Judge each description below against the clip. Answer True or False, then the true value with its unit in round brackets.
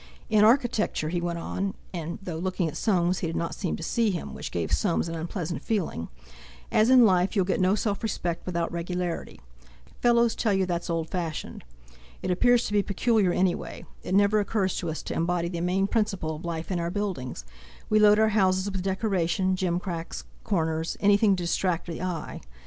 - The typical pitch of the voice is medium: True (180 Hz)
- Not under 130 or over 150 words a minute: False (190 wpm)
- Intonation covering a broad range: False (3.3 semitones)